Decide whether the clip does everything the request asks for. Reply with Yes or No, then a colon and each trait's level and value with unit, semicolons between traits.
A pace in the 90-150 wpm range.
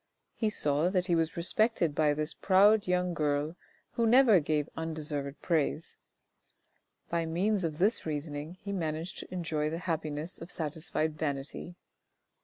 Yes: average, 145 wpm